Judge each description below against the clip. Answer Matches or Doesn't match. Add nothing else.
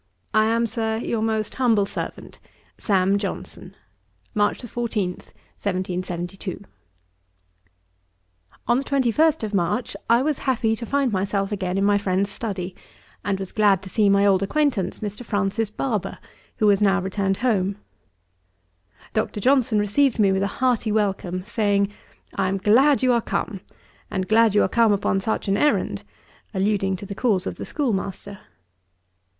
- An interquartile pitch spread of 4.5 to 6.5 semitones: Doesn't match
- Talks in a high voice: Matches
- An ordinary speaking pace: Matches